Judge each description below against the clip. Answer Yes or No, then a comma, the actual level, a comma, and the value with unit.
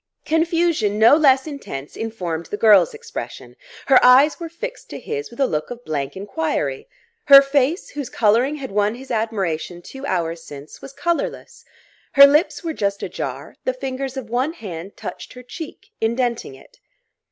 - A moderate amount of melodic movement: No, wide, 6.8 semitones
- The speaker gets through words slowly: No, average, 165 wpm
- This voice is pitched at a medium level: No, very high, 255 Hz